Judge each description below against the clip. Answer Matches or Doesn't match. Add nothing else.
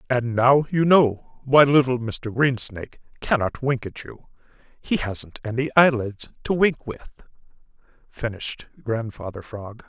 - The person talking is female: Doesn't match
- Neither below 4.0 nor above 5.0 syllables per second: Matches